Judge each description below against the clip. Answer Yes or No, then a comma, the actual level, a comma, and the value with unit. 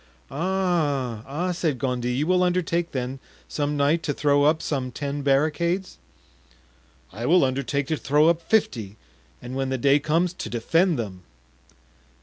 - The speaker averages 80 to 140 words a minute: No, average, 150 wpm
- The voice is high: No, medium, 145 Hz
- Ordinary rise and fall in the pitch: Yes, average, 4.4 semitones